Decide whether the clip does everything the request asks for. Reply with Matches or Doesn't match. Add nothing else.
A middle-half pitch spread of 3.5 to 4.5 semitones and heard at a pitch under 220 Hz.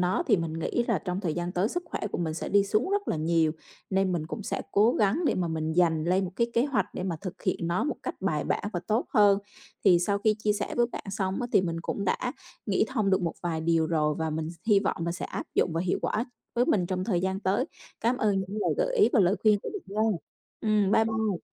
Matches